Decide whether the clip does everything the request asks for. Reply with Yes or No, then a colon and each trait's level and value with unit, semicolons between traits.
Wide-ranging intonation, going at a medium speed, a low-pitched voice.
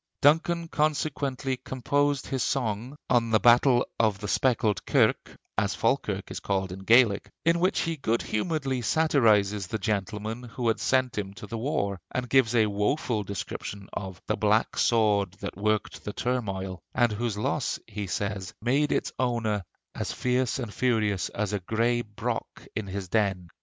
No: average, 4.1 semitones; average, 165 wpm; low, 115 Hz